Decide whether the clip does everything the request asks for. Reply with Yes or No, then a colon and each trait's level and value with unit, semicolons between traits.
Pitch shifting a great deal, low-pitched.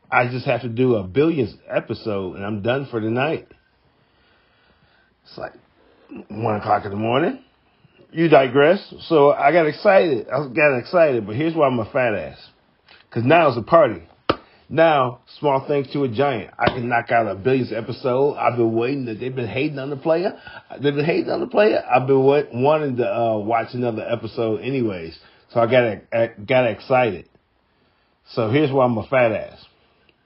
No: average, 3.8 semitones; low, 125 Hz